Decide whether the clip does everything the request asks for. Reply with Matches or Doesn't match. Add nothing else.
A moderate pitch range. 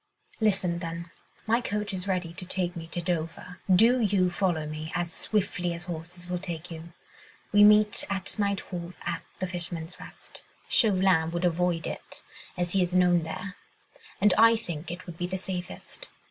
Doesn't match